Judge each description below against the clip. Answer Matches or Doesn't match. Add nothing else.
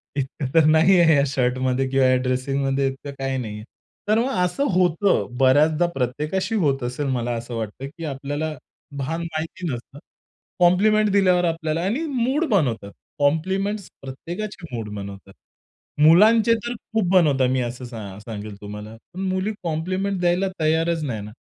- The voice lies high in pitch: Doesn't match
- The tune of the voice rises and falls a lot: Matches